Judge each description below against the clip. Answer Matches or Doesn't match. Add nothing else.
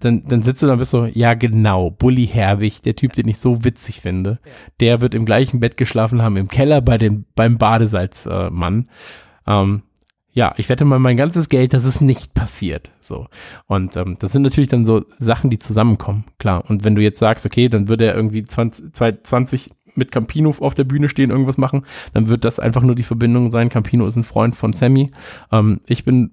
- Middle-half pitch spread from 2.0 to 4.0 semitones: Matches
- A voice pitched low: Matches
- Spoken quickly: Matches